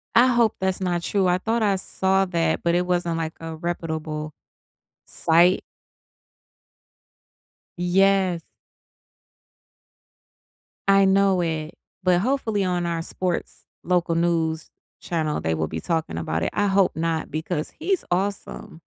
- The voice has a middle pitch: Yes, medium, 175 Hz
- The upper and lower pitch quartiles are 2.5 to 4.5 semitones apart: Yes, average, 2.9 semitones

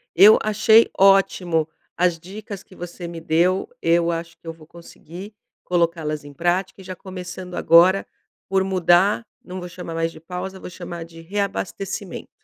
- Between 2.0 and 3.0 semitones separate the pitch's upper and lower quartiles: Yes, narrow, 2.4 semitones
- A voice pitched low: No, medium, 180 Hz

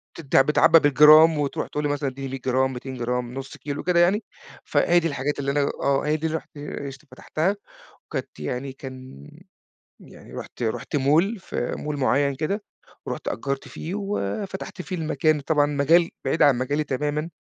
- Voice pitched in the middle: Yes, medium, 145 Hz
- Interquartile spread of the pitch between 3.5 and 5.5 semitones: No, average, 3.1 semitones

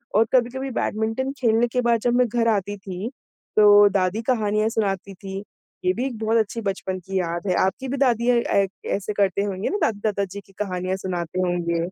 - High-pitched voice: Yes, high, 205 Hz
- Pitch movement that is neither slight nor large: Yes, average, 3.4 semitones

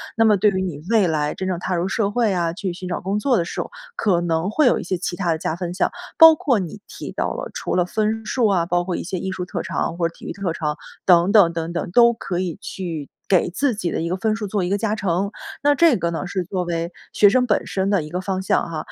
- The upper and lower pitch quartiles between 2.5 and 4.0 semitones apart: Yes, average, 3.4 semitones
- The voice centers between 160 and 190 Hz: Yes, medium, 185 Hz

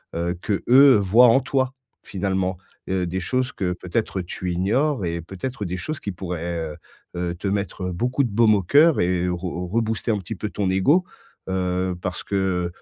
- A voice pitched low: Yes, very low, 95 Hz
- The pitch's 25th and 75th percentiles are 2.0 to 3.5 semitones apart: No, average, 4.3 semitones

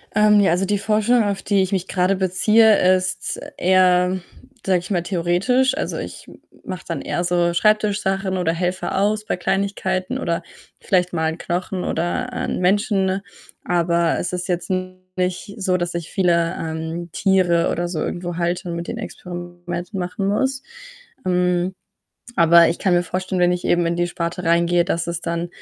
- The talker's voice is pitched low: No, medium, 180 Hz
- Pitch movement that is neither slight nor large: No, narrow, 2.0 semitones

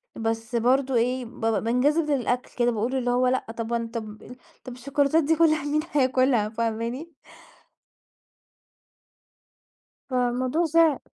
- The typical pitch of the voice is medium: No, very high, 250 Hz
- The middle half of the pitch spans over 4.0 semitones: No, average, 3.3 semitones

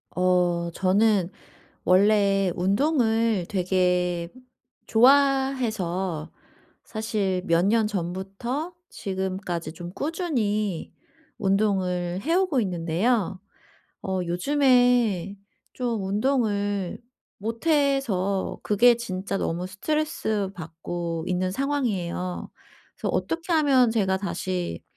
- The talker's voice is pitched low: No, high, 200 Hz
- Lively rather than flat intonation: No, average, 5.0 semitones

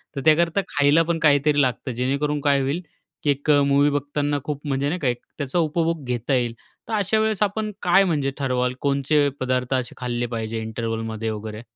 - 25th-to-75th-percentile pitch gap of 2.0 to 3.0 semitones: No, average, 3.7 semitones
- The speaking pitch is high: No, medium, 140 Hz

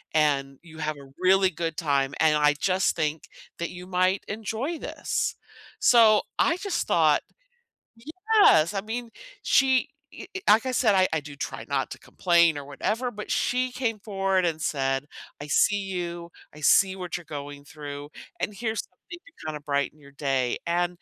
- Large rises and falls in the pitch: Yes, wide, 6.1 semitones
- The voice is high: No, medium, 175 Hz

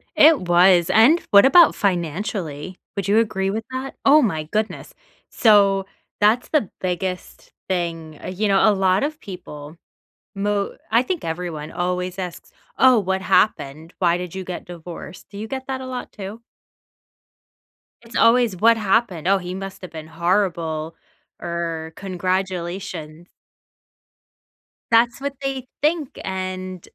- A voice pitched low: No, high, 190 Hz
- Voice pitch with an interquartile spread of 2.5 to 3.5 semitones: No, average, 4.3 semitones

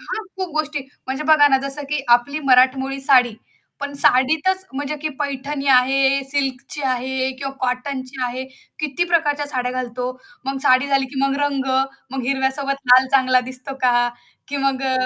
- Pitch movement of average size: No, narrow, 1.8 semitones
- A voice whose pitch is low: No, very high, 270 Hz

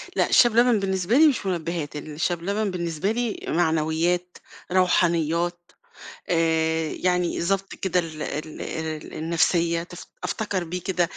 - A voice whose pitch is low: No, medium, 175 Hz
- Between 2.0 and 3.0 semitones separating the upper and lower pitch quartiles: Yes, average, 2.7 semitones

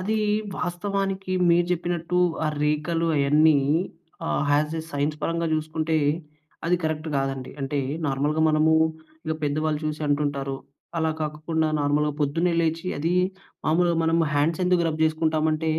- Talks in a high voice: No, medium, 155 Hz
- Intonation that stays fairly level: Yes, narrow, 2.0 semitones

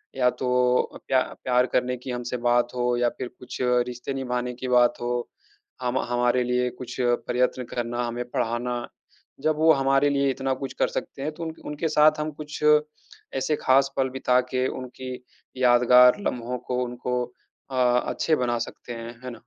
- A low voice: Yes, low, 125 Hz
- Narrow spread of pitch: Yes, narrow, 1.5 semitones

